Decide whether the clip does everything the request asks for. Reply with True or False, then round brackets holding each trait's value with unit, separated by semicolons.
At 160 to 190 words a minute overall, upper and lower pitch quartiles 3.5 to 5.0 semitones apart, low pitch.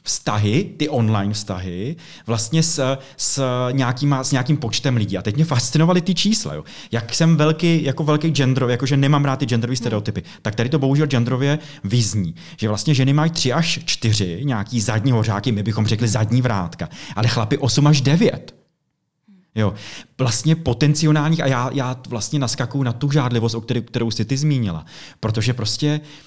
True (170 wpm; 4.6 semitones; 130 Hz)